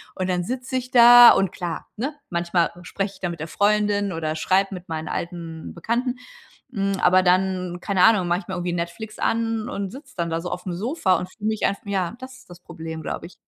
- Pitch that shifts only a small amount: No, average, 4.0 semitones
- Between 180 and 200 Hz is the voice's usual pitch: Yes, medium, 185 Hz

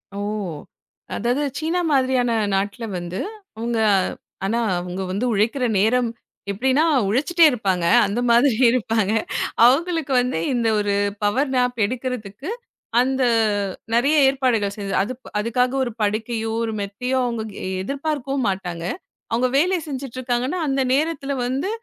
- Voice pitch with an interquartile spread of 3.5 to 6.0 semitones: Yes, average, 4.2 semitones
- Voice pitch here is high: Yes, high, 245 Hz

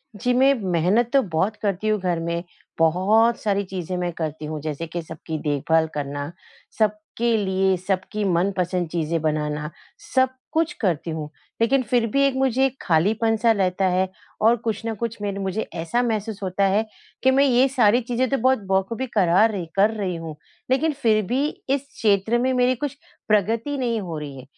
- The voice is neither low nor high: No, high, 205 Hz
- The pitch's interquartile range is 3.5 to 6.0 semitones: Yes, wide, 5.6 semitones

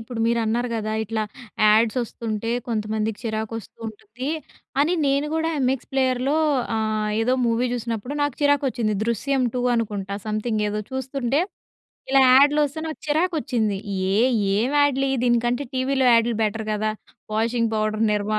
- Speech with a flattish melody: No, average, 3.5 semitones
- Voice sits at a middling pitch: No, high, 235 Hz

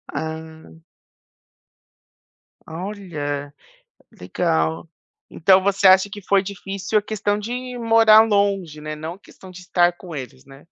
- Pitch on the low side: No, medium, 185 Hz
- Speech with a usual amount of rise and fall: Yes, average, 4.3 semitones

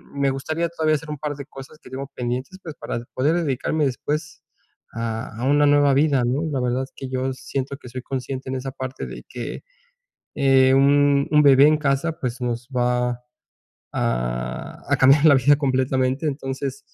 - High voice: No, low, 135 Hz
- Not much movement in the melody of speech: Yes, narrow, 2.0 semitones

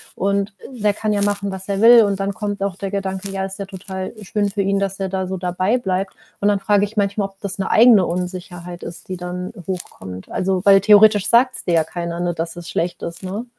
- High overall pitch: Yes, high, 195 Hz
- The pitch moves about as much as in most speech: No, narrow, 1.9 semitones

